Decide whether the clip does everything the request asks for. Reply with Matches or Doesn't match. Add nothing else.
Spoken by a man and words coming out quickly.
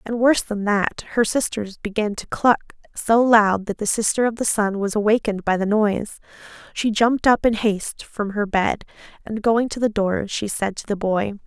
Doesn't match